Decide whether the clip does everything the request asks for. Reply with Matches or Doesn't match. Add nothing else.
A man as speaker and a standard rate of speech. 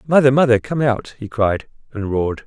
Matches